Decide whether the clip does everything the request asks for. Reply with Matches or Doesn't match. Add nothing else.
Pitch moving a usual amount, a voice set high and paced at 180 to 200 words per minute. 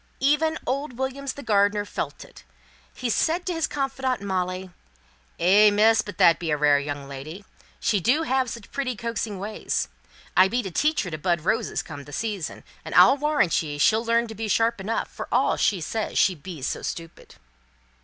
Doesn't match